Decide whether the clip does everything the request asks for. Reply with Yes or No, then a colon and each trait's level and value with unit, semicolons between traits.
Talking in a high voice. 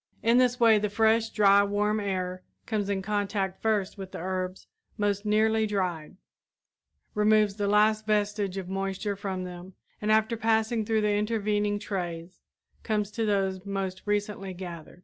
Yes: high, 205 Hz